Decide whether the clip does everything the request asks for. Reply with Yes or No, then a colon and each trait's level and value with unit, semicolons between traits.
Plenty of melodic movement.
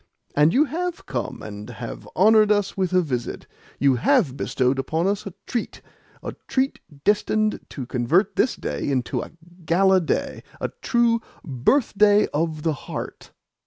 Yes: wide, 7.1 semitones